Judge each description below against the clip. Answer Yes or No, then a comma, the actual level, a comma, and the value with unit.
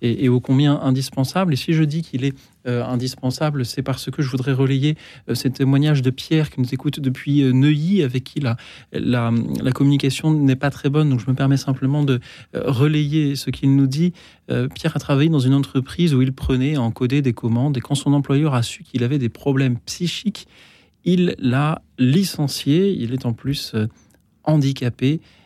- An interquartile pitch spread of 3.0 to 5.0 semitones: No, narrow, 2.4 semitones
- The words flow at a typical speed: Yes, average, 205 wpm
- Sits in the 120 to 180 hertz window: Yes, low, 135 Hz